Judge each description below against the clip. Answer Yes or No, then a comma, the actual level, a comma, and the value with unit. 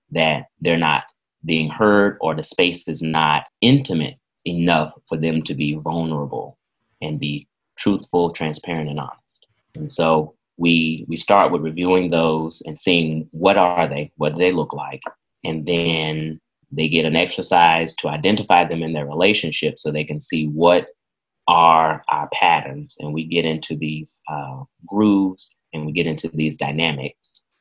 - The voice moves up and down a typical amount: No, narrow, 1.8 semitones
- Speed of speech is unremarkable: Yes, average, 160 wpm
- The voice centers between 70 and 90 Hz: Yes, very low, 80 Hz